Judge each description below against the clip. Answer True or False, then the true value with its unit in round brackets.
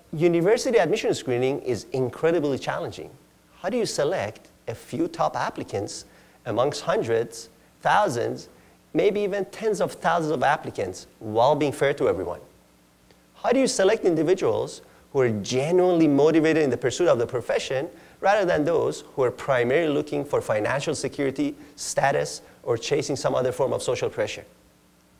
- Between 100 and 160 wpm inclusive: True (150 wpm)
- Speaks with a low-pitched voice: False (155 Hz)